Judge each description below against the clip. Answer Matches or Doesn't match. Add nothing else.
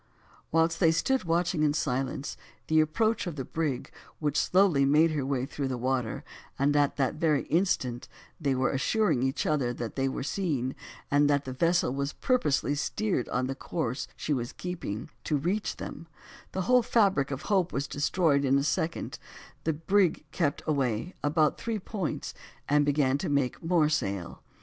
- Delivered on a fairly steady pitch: Doesn't match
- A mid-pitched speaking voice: Matches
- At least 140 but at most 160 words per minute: Doesn't match